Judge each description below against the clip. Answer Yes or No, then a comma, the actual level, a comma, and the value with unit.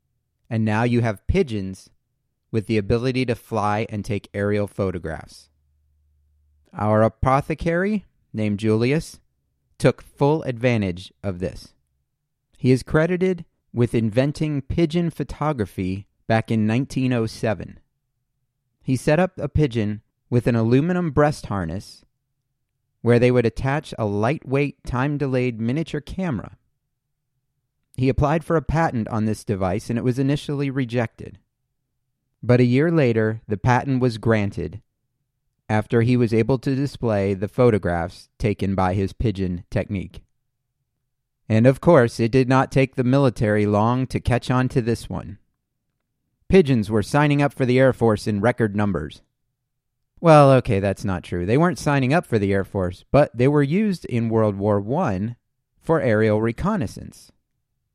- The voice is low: Yes, low, 120 Hz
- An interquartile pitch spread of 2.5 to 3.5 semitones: No, average, 4.3 semitones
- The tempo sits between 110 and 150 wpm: Yes, average, 145 wpm